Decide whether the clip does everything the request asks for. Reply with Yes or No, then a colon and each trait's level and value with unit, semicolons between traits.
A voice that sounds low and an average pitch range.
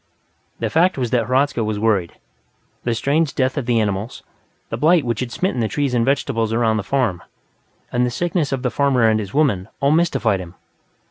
Yes: low, 125 Hz; average, 4.2 semitones